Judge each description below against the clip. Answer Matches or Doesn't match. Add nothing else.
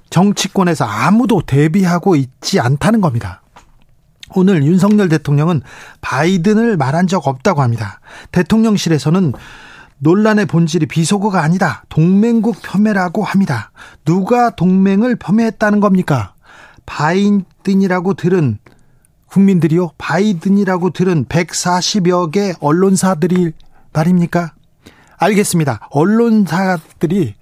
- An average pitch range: Matches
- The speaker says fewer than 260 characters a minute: Doesn't match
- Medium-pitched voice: Matches